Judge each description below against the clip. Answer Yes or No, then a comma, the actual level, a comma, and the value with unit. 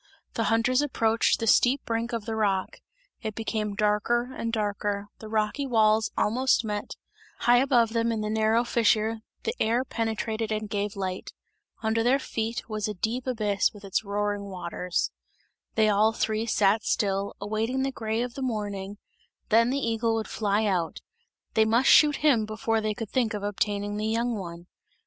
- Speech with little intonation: Yes, narrow, 2.0 semitones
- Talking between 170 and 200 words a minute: Yes, average, 175 wpm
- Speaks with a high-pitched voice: Yes, high, 220 Hz